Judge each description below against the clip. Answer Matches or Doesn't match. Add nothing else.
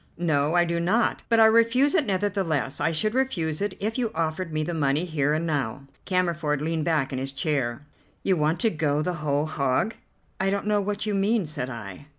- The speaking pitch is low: Doesn't match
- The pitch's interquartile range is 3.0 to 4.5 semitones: Doesn't match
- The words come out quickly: Matches